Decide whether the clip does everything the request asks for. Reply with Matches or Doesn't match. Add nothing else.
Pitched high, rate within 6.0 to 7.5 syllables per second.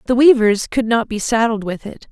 Doesn't match